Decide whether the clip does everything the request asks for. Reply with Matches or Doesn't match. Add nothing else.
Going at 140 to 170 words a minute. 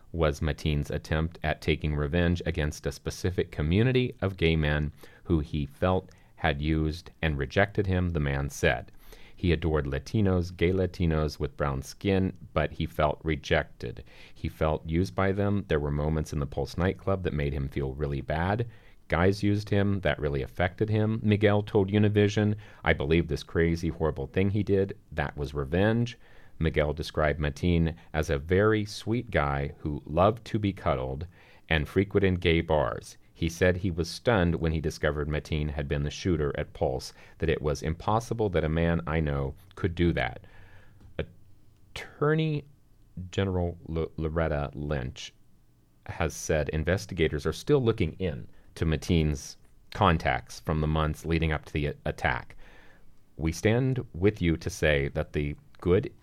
Matches